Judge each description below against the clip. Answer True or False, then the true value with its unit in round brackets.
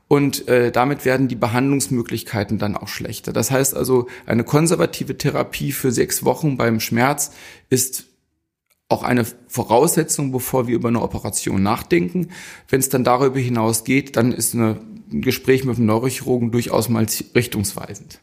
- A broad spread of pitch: False (2.8 semitones)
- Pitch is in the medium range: False (125 Hz)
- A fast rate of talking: False (155 wpm)